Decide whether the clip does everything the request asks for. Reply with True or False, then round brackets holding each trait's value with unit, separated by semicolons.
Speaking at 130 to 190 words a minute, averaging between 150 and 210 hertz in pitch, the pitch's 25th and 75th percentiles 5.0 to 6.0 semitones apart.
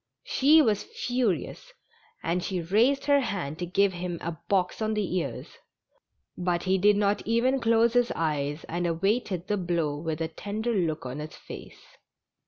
True (165 wpm; 190 Hz; 5.4 semitones)